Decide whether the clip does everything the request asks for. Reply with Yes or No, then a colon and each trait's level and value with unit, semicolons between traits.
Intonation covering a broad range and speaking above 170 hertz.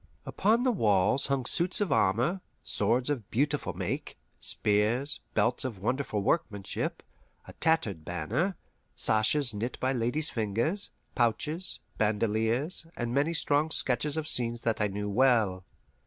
No: wide, 6.0 semitones; low, 120 Hz